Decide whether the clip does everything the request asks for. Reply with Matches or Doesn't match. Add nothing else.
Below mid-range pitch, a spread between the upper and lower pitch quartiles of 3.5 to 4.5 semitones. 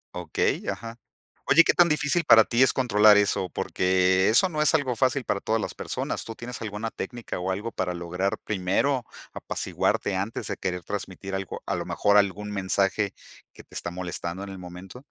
Matches